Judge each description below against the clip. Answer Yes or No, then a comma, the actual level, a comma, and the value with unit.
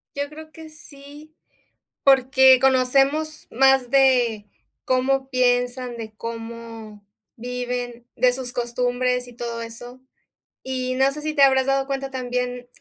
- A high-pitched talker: Yes, very high, 255 Hz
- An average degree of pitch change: No, narrow, 1.7 semitones